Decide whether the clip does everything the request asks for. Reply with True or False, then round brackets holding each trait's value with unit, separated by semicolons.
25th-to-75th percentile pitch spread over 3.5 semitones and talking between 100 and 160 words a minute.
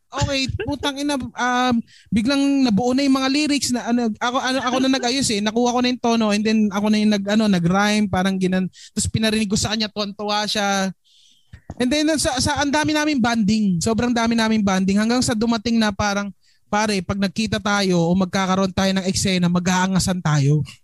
False (4.2 semitones; 195 wpm)